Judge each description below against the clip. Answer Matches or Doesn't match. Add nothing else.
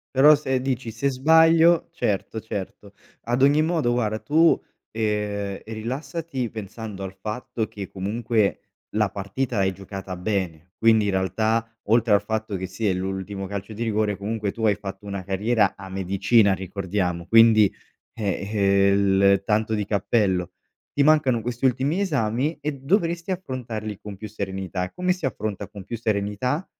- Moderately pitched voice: Doesn't match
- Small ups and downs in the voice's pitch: Doesn't match